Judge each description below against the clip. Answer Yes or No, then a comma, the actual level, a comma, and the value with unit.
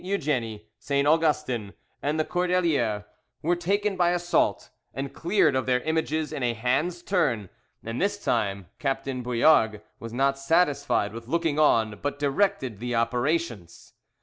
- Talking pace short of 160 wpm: Yes, average, 145 wpm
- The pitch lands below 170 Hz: Yes, medium, 140 Hz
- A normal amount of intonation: No, wide, 6.2 semitones